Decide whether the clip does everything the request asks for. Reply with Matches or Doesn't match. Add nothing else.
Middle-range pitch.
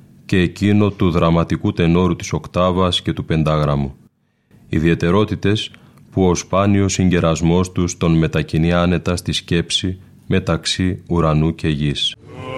Doesn't match